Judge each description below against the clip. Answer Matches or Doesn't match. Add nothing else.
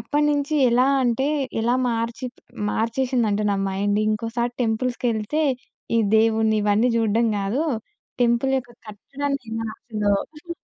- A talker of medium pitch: Doesn't match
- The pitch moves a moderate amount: Matches